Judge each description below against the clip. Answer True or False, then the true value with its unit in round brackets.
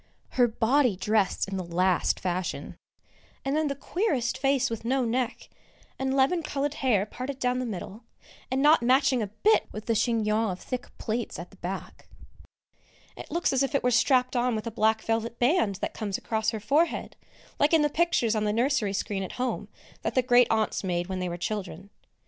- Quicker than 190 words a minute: True (200 wpm)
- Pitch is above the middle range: True (235 Hz)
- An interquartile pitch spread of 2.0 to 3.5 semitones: False (4.2 semitones)